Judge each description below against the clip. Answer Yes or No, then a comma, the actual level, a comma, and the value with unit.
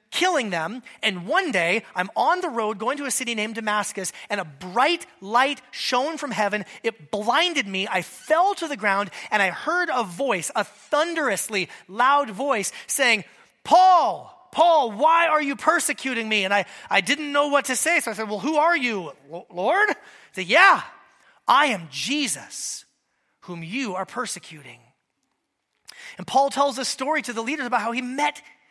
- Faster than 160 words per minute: Yes, average, 180 wpm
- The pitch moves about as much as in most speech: No, wide, 6.5 semitones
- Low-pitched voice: No, high, 245 Hz